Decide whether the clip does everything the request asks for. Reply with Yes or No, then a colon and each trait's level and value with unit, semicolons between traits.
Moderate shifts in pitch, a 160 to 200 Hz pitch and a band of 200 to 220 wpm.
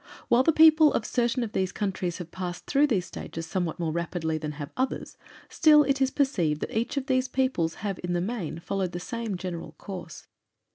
No: wide, 7.0 semitones; high, 190 Hz; fast, 205 wpm